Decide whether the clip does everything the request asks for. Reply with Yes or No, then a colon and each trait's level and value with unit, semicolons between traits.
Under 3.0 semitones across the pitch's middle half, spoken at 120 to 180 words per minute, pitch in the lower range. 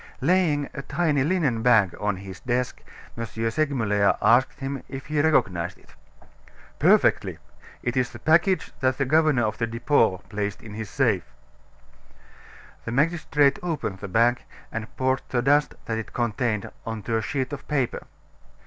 No: average, 4.5 semitones; average, 160 wpm; low, 125 Hz